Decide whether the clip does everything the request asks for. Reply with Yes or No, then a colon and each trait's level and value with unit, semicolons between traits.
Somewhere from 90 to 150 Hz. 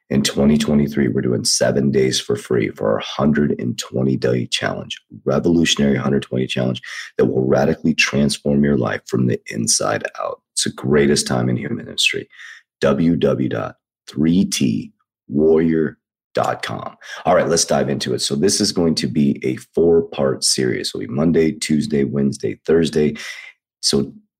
No: very low, 70 Hz